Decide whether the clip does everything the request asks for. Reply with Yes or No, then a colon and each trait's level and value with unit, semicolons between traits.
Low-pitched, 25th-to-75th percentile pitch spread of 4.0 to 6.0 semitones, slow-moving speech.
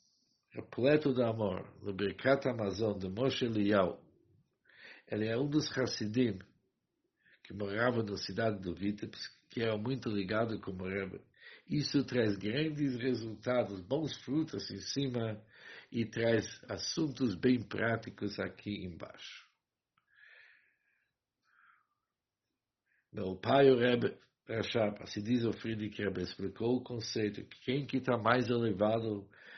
No: low, 115 Hz; average, 3.6 semitones; slow, 120 wpm